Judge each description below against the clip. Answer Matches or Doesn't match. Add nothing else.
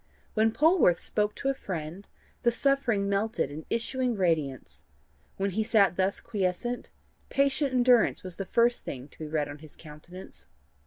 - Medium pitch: Doesn't match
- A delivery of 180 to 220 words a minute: Doesn't match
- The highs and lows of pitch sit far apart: Matches